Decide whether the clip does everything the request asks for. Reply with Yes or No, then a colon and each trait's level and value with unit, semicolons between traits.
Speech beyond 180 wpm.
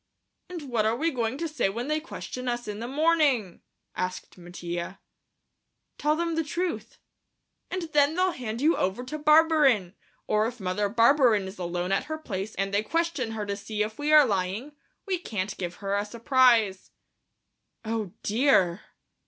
No: average, 170 wpm